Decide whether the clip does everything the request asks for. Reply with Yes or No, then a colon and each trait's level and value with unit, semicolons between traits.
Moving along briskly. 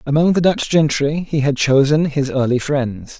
No: average, 190 wpm